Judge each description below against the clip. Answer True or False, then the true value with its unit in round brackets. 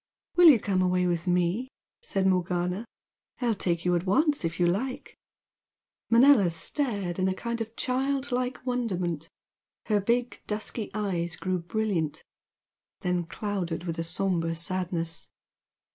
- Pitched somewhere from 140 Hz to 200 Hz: True (190 Hz)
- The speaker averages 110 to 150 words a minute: True (140 wpm)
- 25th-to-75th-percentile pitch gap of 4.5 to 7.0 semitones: True (5.2 semitones)